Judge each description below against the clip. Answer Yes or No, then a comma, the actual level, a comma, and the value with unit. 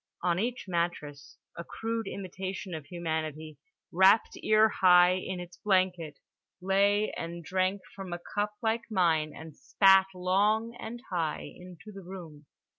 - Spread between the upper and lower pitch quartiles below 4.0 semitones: Yes, average, 2.9 semitones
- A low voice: No, medium, 185 Hz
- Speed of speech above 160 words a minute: No, average, 140 wpm